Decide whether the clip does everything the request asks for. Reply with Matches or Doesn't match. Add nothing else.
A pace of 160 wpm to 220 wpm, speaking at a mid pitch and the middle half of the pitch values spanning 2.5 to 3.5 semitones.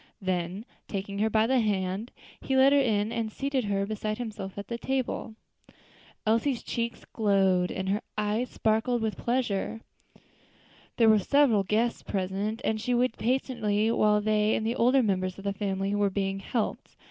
Doesn't match